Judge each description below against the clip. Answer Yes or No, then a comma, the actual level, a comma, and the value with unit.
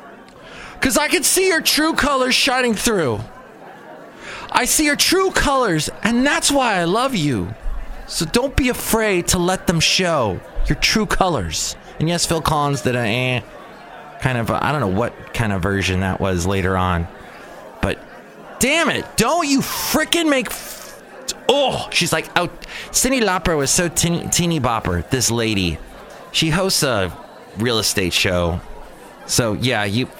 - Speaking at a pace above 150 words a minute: Yes, average, 165 wpm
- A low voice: No, medium, 170 Hz